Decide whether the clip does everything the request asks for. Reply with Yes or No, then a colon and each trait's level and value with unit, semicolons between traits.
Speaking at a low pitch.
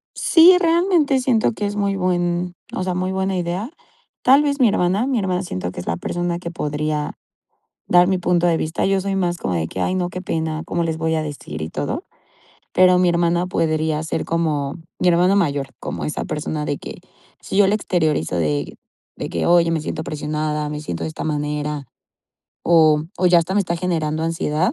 No: medium, 170 Hz